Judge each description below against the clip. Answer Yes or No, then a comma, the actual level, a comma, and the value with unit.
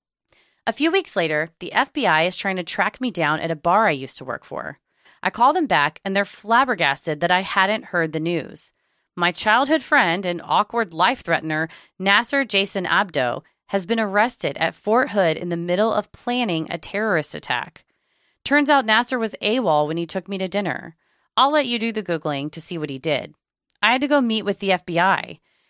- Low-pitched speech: No, high, 195 Hz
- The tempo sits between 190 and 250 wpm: Yes, fast, 205 wpm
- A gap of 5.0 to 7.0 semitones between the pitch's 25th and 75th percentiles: Yes, wide, 5.4 semitones